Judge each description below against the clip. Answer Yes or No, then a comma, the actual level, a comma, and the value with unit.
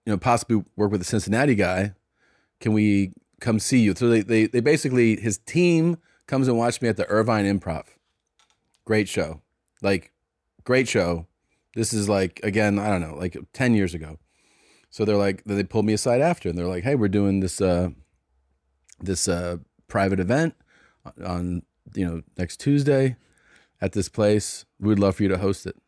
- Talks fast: No, average, 185 wpm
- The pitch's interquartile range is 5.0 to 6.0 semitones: No, average, 4.1 semitones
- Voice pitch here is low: Yes, low, 105 Hz